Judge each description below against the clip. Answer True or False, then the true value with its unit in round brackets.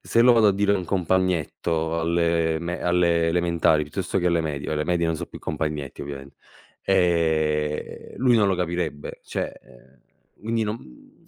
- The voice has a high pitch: False (85 Hz)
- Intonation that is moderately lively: True (3.1 semitones)